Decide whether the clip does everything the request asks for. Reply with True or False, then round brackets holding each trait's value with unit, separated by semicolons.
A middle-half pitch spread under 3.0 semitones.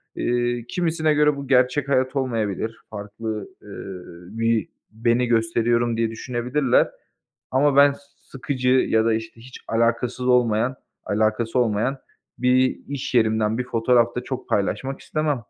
True (2.5 semitones)